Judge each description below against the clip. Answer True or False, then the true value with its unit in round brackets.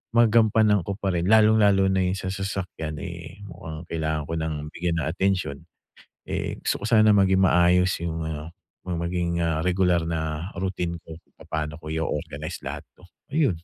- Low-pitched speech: True (90 Hz)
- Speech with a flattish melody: False (3.3 semitones)